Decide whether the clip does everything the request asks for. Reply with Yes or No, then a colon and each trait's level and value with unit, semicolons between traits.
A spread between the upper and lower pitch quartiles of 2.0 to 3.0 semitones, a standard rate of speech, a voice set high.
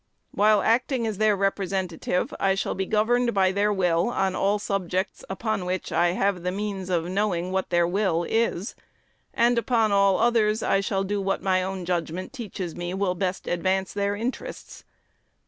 Yes: narrow, 2.5 semitones; average, 175 wpm; high, 195 Hz